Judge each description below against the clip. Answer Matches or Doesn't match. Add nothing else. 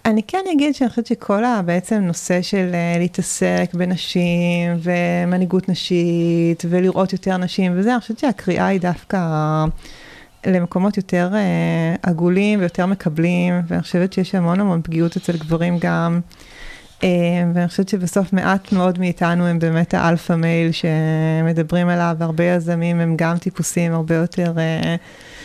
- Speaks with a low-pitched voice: Doesn't match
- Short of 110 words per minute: Doesn't match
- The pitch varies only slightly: Matches